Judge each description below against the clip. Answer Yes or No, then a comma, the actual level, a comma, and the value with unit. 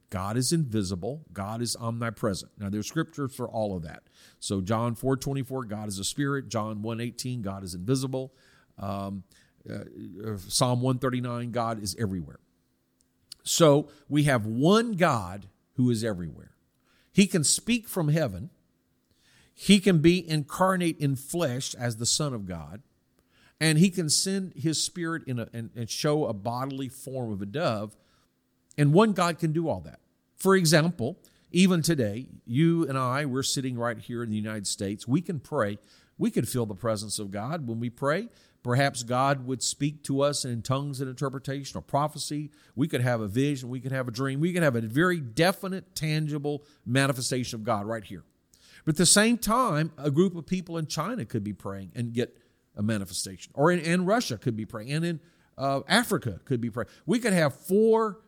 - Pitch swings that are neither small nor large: No, wide, 5.9 semitones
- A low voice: Yes, low, 130 Hz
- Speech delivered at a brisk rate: No, average, 180 wpm